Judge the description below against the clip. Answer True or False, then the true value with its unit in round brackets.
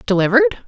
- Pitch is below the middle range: False (220 Hz)